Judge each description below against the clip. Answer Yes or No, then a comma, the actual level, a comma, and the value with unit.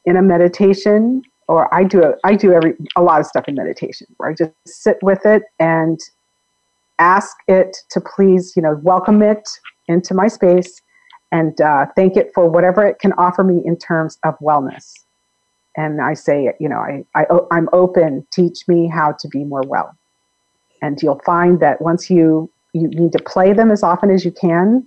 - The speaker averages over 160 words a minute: Yes, average, 195 wpm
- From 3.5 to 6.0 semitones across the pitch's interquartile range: No, average, 2.9 semitones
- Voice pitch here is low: No, medium, 175 Hz